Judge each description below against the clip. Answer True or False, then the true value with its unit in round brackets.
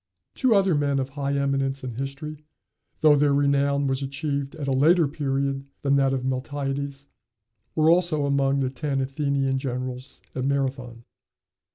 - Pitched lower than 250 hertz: True (140 Hz)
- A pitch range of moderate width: False (1.1 semitones)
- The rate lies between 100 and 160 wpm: True (155 wpm)